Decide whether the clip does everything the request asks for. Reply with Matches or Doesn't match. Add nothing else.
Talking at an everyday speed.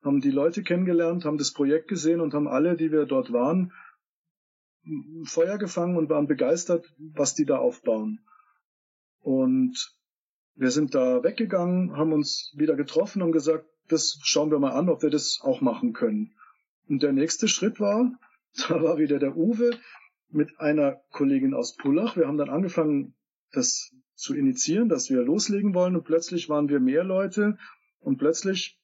Matches